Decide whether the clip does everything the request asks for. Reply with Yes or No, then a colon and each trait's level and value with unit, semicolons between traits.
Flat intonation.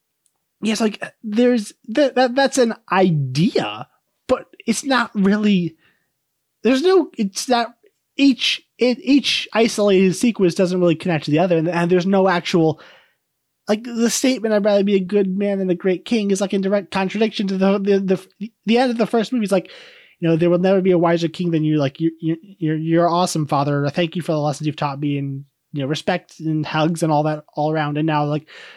No: wide, 5.5 semitones